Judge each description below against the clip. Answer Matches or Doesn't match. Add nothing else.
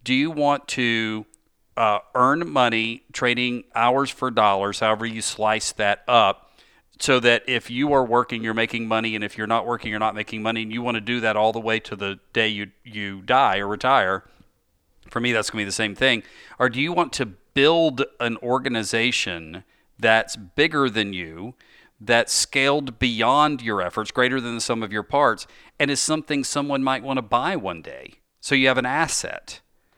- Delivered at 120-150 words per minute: Doesn't match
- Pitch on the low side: Matches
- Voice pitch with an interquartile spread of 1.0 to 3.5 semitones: Matches